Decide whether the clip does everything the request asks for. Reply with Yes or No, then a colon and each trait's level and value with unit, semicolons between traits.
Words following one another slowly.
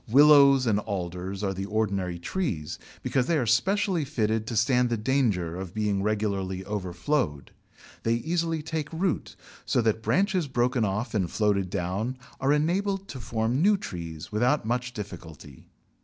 No: average, 155 wpm